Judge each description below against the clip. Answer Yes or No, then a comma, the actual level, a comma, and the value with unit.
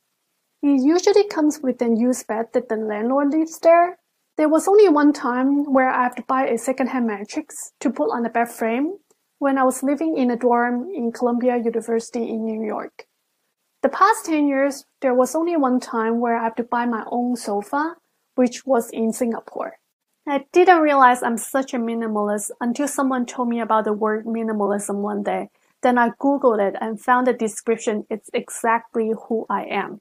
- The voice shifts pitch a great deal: No, average, 3.7 semitones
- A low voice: No, high, 245 Hz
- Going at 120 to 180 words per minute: No, average, 190 wpm